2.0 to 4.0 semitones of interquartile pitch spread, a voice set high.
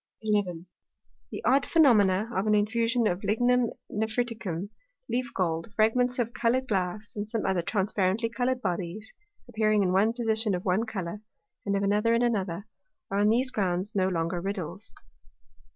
Yes: average, 3.5 semitones; high, 210 Hz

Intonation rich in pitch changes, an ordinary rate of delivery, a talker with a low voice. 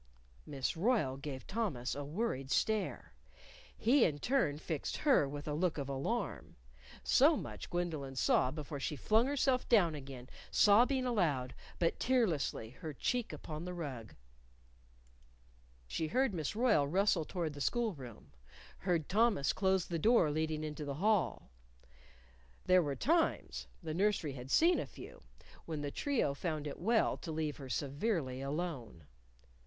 No: wide, 7.1 semitones; average, 150 wpm; medium, 160 Hz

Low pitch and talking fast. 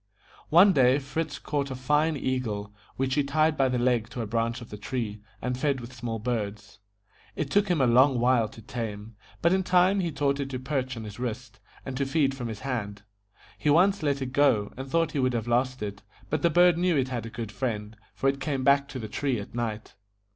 Yes: low, 130 Hz; fast, 235 wpm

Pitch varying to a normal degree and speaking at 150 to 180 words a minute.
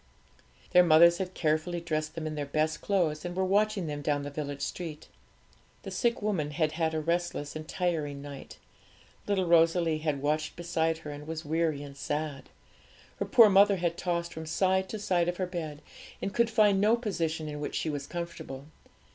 No: average, 3.0 semitones; average, 190 wpm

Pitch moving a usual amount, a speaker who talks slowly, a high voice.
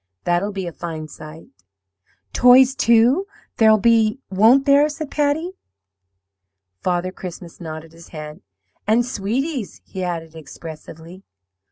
No: wide, 7.3 semitones; slow, 115 wpm; high, 195 Hz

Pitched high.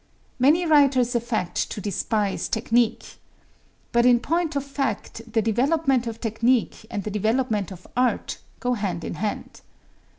Yes: high, 235 Hz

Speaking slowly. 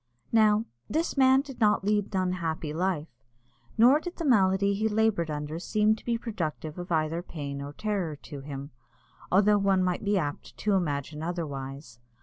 No: average, 170 wpm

